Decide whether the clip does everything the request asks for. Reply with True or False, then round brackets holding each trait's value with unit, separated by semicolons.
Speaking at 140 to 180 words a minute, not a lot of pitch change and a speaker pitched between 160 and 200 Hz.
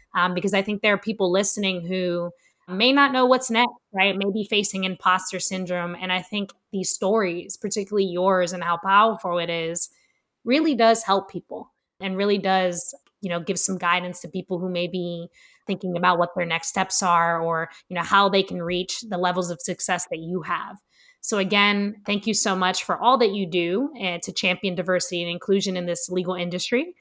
False (200 wpm; 2.3 semitones; 185 Hz)